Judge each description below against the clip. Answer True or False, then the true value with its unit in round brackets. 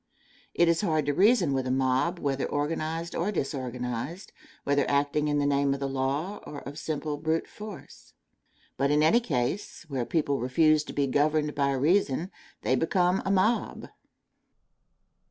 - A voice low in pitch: False (150 Hz)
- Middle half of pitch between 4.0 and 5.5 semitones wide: False (3.4 semitones)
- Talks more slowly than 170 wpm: True (160 wpm)